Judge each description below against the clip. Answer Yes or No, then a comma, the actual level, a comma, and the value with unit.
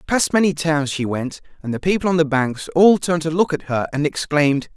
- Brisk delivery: Yes, fast, 240 wpm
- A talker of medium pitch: Yes, medium, 155 Hz